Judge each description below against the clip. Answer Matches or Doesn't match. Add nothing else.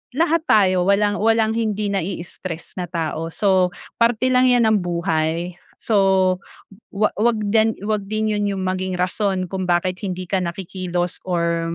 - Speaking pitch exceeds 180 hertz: Matches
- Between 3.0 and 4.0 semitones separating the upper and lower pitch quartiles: Matches